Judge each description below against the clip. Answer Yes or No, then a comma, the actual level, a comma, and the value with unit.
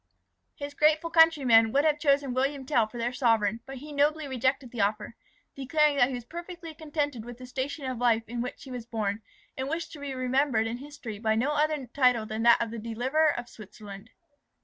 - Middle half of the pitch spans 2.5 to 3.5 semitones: No, average, 4.0 semitones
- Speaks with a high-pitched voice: Yes, very high, 255 Hz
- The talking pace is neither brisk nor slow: No, fast, 210 wpm